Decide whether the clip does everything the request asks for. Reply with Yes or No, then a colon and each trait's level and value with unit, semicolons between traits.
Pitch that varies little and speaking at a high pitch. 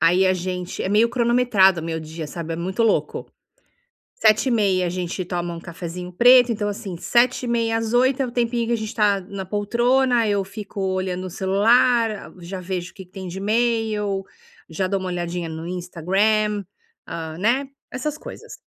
No: average, 4.3 semitones; high, 195 Hz